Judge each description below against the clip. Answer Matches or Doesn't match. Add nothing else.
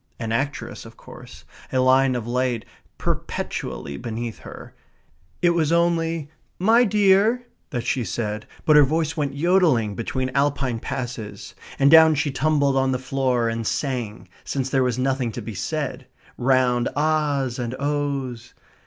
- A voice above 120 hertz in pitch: Matches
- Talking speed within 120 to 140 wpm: Doesn't match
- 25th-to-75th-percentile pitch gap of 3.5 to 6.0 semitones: Matches